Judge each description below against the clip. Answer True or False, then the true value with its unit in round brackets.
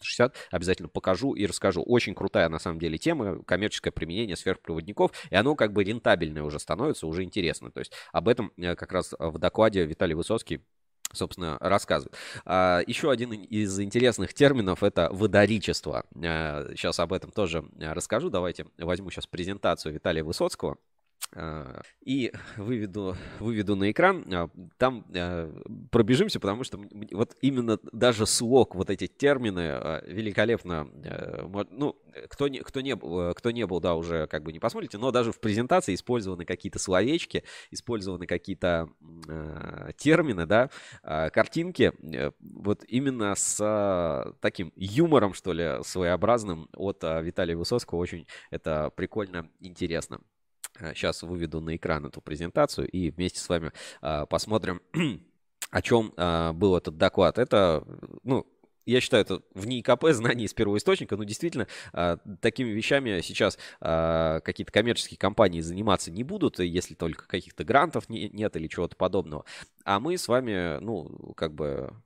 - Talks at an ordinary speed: True (140 wpm)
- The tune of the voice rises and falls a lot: False (4.8 semitones)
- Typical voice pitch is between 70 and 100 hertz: True (95 Hz)